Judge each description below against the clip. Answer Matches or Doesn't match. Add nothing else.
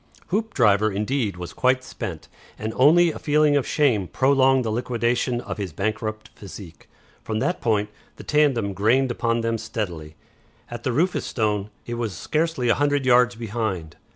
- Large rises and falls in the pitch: Doesn't match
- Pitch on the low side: Matches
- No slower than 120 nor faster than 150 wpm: Doesn't match